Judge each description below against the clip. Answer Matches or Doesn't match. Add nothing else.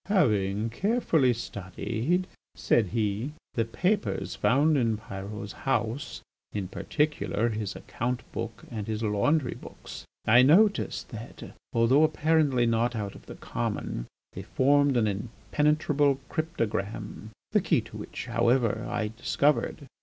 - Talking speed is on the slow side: Matches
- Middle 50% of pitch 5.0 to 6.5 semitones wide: Matches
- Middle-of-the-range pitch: Doesn't match